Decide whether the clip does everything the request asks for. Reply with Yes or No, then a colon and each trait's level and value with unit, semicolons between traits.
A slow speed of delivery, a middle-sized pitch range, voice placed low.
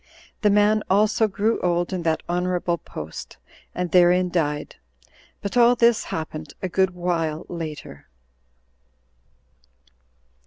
No: slow, 115 wpm; average, 3.6 semitones; medium, 180 Hz